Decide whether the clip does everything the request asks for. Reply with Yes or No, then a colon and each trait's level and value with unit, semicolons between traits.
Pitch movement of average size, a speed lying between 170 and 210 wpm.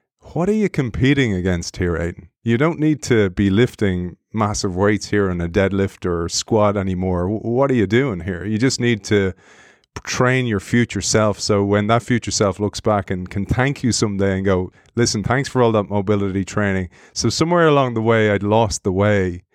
Yes: average, 3.5 semitones; average, 200 wpm